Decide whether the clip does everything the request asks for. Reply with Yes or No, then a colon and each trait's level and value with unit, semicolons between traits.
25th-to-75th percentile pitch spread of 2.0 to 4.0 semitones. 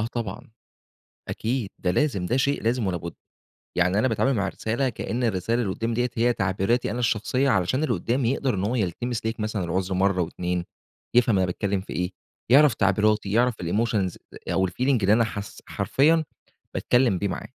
No: average, 4.5 semitones